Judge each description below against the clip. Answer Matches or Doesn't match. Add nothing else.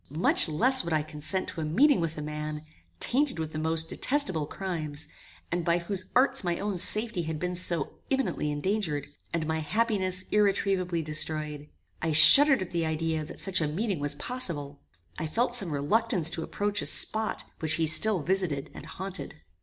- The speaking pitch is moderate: Matches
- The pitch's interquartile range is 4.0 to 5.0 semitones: Matches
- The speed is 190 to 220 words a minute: Doesn't match